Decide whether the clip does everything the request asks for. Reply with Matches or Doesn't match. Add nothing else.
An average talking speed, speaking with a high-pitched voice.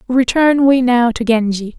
Matches